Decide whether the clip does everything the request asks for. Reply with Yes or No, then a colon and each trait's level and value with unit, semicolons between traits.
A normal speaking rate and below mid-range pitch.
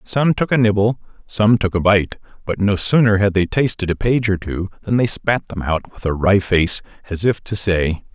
No: fast, 230 wpm; low, 100 Hz